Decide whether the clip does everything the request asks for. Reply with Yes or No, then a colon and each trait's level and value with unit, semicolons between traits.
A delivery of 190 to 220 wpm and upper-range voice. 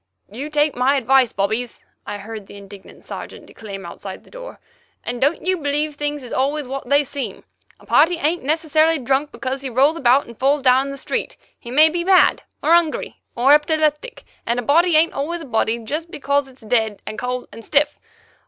Yes: average, 200 wpm; very high, 280 Hz